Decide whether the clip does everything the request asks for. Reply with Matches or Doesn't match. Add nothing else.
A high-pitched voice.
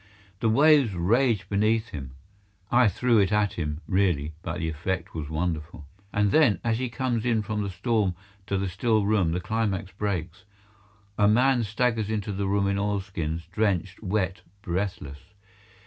Doesn't match